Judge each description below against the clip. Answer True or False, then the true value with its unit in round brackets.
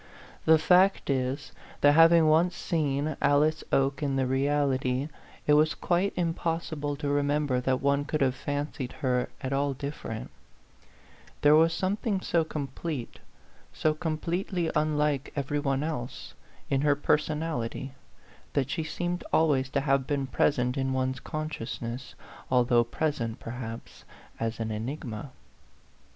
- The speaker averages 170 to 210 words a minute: False (140 wpm)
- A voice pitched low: False (145 Hz)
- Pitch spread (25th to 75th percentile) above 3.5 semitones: False (3.0 semitones)